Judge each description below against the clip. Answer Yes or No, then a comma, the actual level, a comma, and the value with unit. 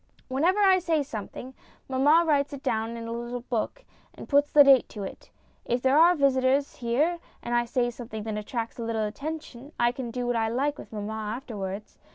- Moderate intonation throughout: Yes, average, 3.8 semitones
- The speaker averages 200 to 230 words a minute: Yes, fast, 205 wpm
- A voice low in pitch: No, high, 245 Hz